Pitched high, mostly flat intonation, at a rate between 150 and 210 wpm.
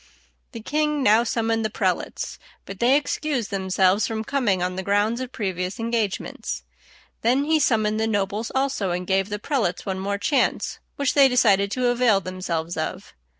No: high, 220 Hz; average, 4.5 semitones; average, 170 wpm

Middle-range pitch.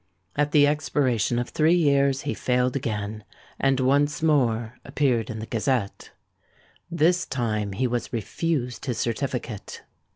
No: low, 130 Hz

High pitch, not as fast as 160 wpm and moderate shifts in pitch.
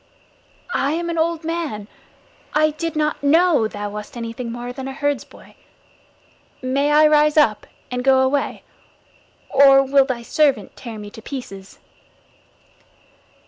Yes: very high, 275 Hz; average, 140 wpm; average, 4.2 semitones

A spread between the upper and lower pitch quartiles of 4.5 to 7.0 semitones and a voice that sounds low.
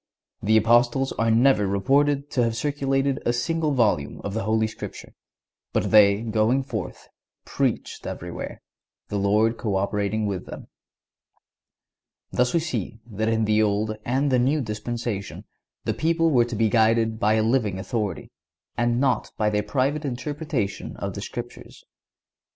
No: average, 3.9 semitones; low, 115 Hz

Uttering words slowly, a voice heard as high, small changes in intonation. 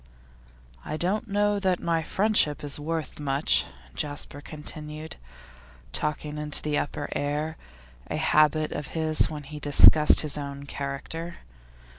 No: slow, 130 wpm; medium, 150 Hz; narrow, 1.8 semitones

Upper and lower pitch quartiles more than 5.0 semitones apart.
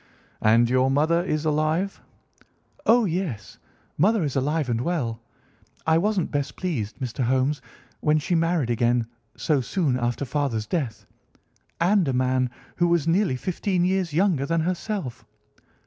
Yes: wide, 5.5 semitones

